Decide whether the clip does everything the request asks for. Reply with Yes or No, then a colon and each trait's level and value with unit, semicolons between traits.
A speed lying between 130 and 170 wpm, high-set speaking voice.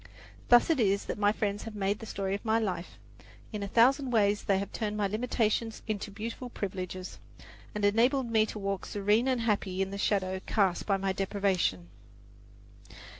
No: average, 180 wpm; high, 205 Hz